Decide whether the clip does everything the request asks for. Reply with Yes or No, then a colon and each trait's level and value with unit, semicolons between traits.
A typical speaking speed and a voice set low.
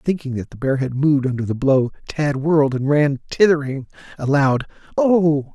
No: average, 185 wpm; medium, 145 Hz